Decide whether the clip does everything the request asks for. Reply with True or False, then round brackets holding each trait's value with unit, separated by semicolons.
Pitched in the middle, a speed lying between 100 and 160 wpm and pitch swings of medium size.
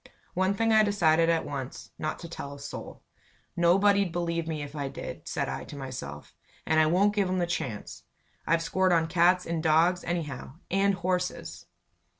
False (170 Hz; 180 wpm; 3.1 semitones)